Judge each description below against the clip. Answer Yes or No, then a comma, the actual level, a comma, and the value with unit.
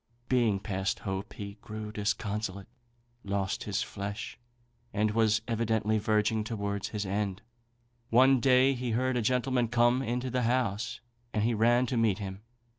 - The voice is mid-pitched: No, low, 110 Hz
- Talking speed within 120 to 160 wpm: Yes, average, 150 wpm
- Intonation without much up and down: No, average, 3.0 semitones